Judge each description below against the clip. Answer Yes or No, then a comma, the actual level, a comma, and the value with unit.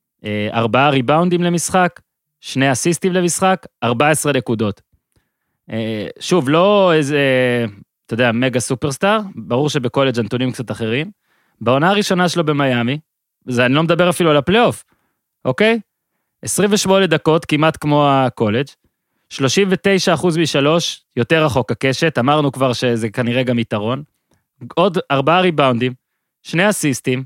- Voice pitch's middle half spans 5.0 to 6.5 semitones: Yes, wide, 5.6 semitones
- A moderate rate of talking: Yes, average, 115 wpm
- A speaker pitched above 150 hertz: No, medium, 145 Hz